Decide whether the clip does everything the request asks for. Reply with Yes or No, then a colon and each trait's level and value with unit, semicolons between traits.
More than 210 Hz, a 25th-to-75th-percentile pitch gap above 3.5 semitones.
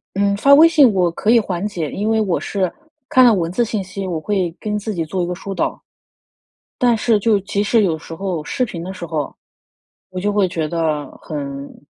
No: high, 195 Hz; average, 4.0 semitones